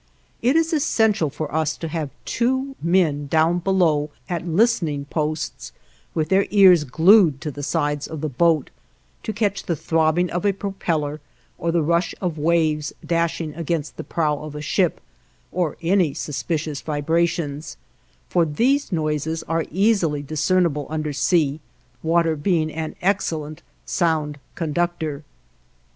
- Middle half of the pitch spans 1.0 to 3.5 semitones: Yes, average, 2.9 semitones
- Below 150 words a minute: Yes, average, 140 wpm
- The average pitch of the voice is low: No, medium, 160 Hz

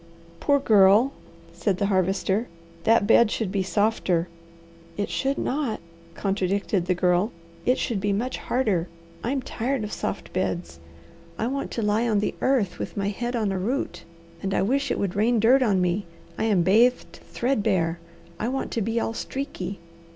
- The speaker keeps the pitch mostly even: No, average, 3.9 semitones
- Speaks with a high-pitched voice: Yes, high, 210 Hz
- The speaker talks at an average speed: Yes, average, 175 wpm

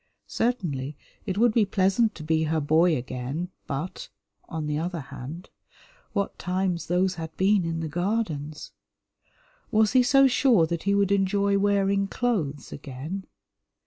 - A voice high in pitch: No, medium, 180 Hz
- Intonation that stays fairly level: No, average, 4.3 semitones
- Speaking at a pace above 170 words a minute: No, average, 145 wpm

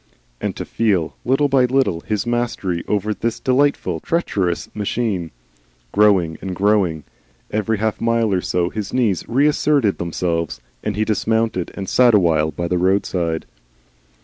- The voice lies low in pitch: Yes, low, 105 Hz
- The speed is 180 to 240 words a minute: No, average, 145 wpm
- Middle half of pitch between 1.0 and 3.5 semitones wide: No, average, 4.7 semitones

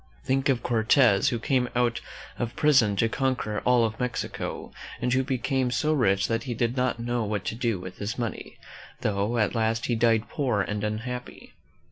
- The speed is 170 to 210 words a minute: Yes, average, 185 wpm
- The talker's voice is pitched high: No, low, 120 Hz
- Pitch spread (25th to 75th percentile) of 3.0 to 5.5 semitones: No, narrow, 2.5 semitones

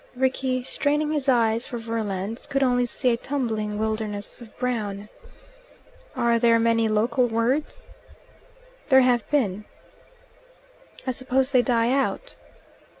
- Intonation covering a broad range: No, average, 2.9 semitones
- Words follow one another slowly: Yes, slow, 125 wpm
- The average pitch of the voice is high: Yes, high, 240 Hz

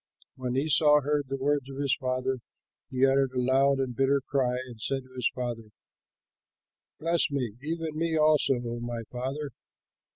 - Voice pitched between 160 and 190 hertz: No, low, 135 Hz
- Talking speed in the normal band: Yes, average, 165 wpm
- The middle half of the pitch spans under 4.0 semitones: Yes, narrow, 2.4 semitones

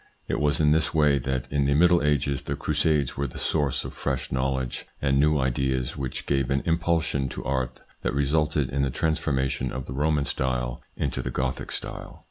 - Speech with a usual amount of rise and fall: No, narrow, 2.3 semitones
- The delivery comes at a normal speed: Yes, average, 195 wpm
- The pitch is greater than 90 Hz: No, very low, 70 Hz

